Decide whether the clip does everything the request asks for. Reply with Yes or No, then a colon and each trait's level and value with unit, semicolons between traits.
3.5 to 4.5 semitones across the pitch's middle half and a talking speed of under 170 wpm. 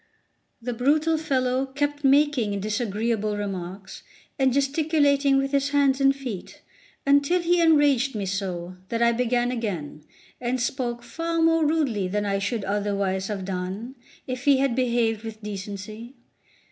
No: average, 5.3 semitones; average, 145 wpm